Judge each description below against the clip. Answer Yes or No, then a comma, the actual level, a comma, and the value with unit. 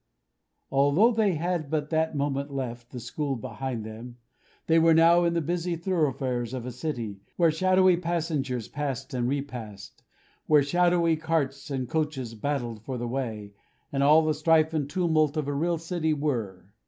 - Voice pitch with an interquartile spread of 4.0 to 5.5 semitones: Yes, average, 4.5 semitones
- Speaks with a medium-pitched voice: Yes, medium, 145 Hz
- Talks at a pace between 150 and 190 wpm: Yes, average, 165 wpm